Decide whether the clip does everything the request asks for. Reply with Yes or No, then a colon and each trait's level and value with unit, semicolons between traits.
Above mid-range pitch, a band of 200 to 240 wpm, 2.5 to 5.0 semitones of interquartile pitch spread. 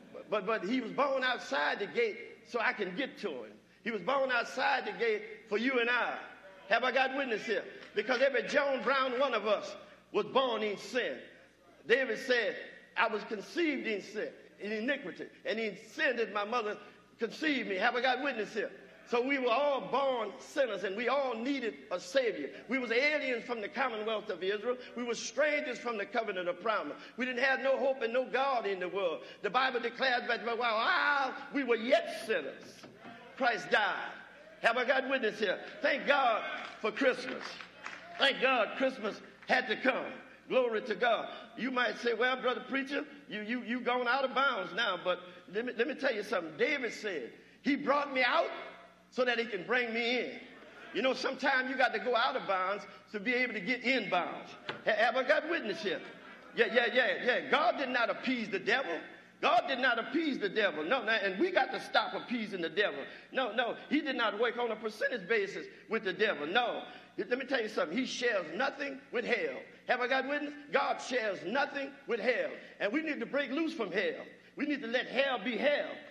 Yes: very high, 255 Hz; fast, 205 wpm; average, 3.7 semitones